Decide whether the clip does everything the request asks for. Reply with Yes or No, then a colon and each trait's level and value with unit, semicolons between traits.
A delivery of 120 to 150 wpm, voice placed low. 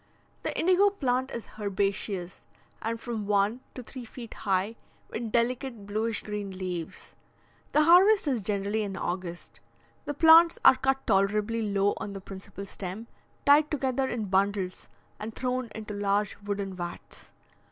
No: average, 145 wpm; high, 215 Hz